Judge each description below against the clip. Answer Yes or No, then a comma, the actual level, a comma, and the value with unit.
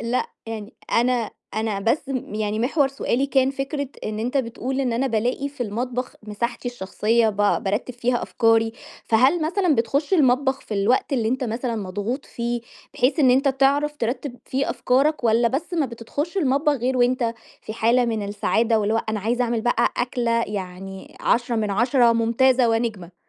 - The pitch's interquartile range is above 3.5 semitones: No, average, 3.1 semitones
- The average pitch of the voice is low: No, high, 240 Hz